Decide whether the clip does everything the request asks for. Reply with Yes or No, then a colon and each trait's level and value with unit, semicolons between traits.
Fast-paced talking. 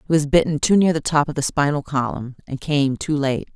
Yes: fast, 255 wpm